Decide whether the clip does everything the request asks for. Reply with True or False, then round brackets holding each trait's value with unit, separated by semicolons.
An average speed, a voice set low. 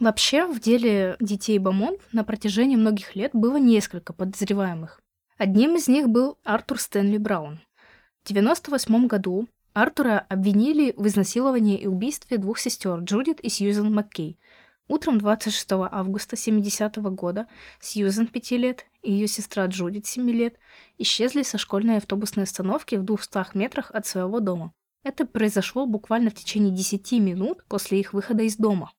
False (145 wpm; 215 Hz)